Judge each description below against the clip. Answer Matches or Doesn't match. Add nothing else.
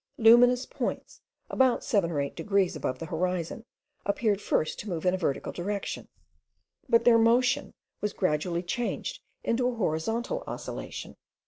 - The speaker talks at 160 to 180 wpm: Doesn't match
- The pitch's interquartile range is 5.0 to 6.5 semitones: Matches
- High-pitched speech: Matches